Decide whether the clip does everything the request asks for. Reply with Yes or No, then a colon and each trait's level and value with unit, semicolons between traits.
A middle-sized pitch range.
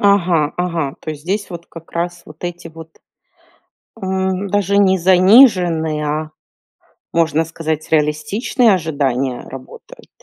Yes: average, 3.3 semitones